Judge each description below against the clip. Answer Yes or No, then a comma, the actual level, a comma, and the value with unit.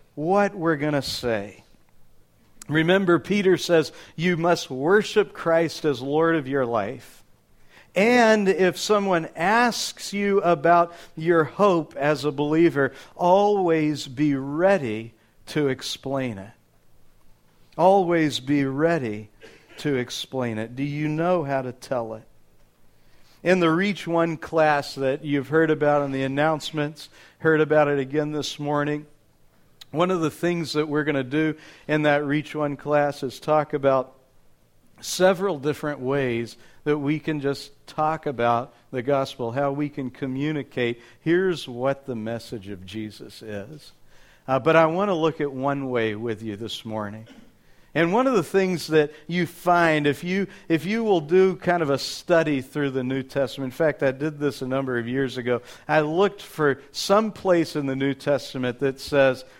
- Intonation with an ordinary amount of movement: Yes, average, 3.9 semitones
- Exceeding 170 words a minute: No, average, 160 wpm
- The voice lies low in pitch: No, medium, 150 Hz